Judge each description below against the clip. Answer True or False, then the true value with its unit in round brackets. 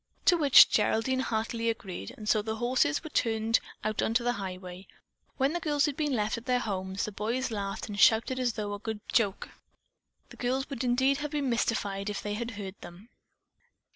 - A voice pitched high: True (225 Hz)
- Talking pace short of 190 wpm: False (200 wpm)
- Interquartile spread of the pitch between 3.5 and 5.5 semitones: True (3.9 semitones)